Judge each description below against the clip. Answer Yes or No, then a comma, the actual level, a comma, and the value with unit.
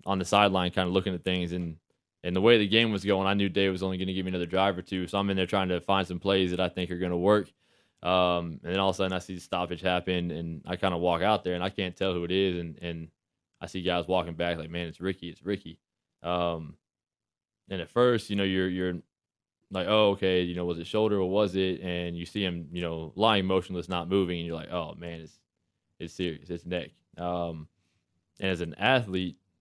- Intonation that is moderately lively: No, narrow, 1.8 semitones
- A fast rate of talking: Yes, fast, 255 wpm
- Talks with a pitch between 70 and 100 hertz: Yes, very low, 90 Hz